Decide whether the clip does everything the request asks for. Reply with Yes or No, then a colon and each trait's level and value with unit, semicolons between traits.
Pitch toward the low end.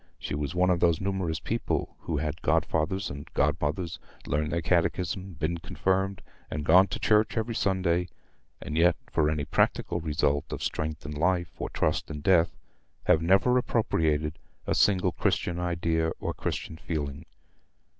Yes: very low, 85 Hz